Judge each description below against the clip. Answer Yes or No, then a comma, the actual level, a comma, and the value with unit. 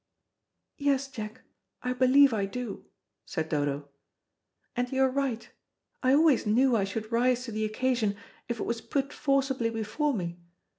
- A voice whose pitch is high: Yes, high, 245 Hz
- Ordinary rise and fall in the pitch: Yes, average, 3.7 semitones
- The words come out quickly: No, average, 155 wpm